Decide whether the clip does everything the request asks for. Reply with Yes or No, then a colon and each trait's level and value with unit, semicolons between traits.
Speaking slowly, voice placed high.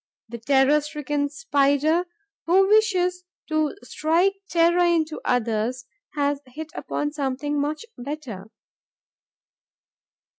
Yes: slow, 100 wpm; very high, 295 Hz